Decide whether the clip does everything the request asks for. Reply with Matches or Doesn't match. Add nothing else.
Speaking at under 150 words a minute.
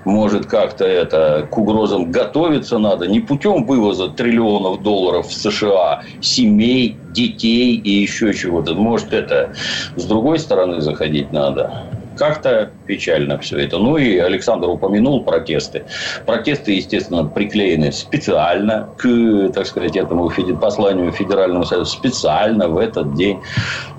Matches